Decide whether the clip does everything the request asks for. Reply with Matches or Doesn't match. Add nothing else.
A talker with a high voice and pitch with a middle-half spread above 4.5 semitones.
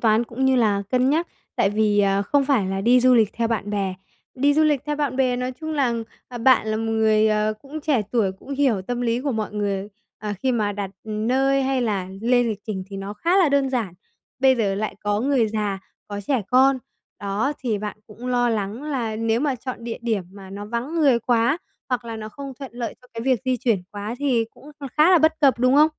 Doesn't match